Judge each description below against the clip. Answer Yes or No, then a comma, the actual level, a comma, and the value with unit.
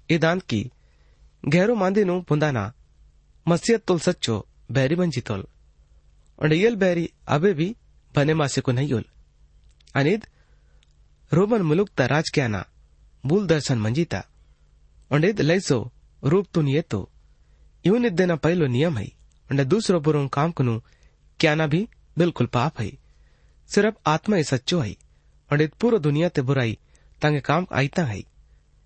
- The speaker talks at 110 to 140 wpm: Yes, average, 115 wpm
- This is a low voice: No, medium, 145 Hz